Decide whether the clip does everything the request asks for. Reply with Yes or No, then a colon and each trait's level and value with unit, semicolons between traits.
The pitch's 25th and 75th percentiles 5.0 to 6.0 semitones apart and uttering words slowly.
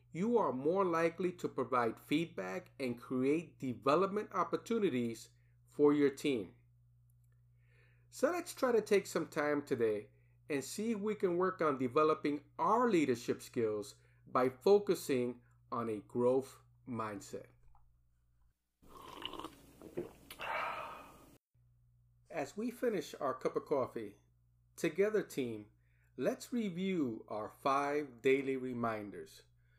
Yes: wide, 5.6 semitones; slow, 110 wpm